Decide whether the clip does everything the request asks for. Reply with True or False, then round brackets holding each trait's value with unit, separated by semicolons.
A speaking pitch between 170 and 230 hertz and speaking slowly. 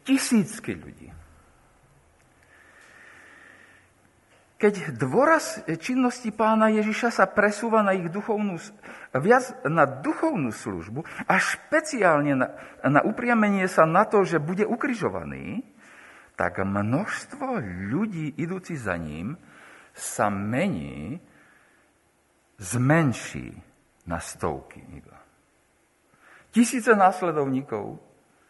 True (185 Hz; 85 wpm)